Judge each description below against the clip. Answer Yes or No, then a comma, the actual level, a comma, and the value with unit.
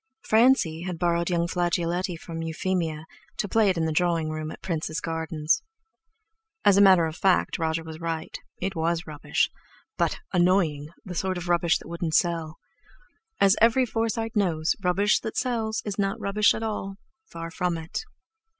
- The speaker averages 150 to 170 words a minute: Yes, average, 160 wpm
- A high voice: No, medium, 175 Hz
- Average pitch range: Yes, average, 3.3 semitones